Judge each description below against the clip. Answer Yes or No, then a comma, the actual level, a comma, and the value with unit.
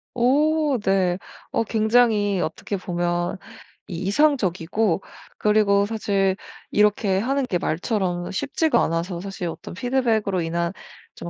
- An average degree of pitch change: Yes, average, 4.3 semitones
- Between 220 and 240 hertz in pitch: No, high, 200 Hz